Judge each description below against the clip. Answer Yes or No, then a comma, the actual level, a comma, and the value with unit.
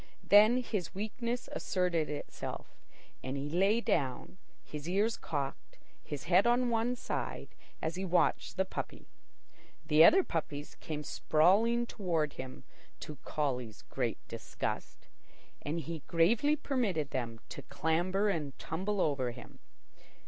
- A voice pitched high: No, medium, 170 Hz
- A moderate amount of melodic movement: No, wide, 6.2 semitones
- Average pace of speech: No, slow, 130 wpm